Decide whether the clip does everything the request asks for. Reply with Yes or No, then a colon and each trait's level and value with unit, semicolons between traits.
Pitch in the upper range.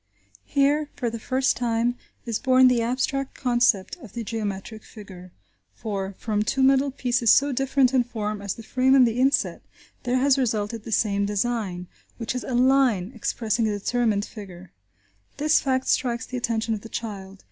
Yes: high, 235 Hz